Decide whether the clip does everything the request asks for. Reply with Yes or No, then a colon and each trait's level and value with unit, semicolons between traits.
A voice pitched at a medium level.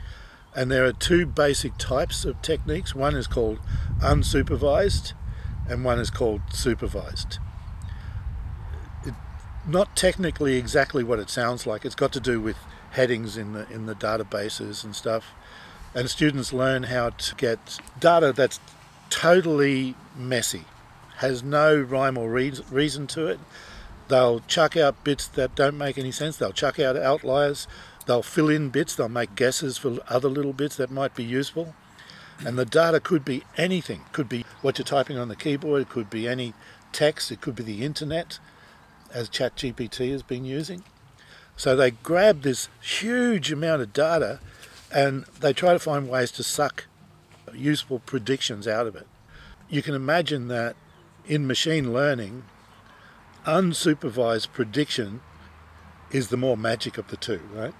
No: low, 130 Hz